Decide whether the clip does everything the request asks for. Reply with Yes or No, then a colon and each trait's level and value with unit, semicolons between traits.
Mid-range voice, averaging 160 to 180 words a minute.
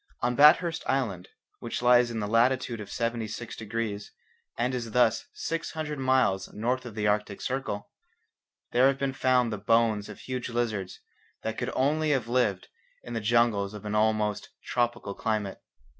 No: low, 115 Hz; average, 165 wpm